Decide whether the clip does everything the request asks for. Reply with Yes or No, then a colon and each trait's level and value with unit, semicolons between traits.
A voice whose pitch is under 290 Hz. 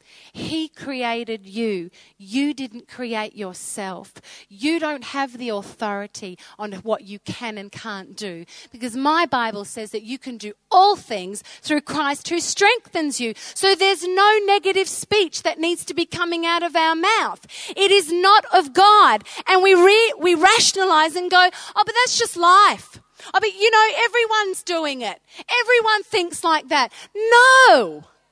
No: very high, 330 Hz